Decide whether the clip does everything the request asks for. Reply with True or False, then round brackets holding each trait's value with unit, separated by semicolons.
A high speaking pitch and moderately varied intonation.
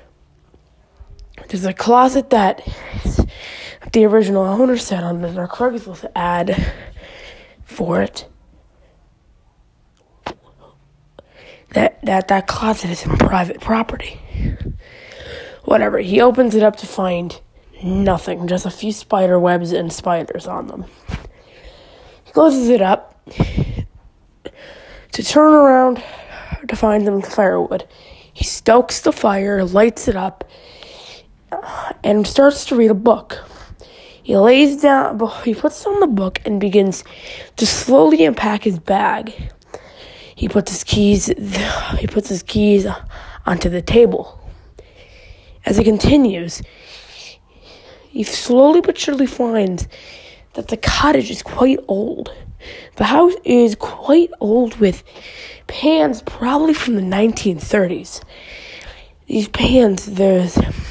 False (220 Hz; 6.7 semitones)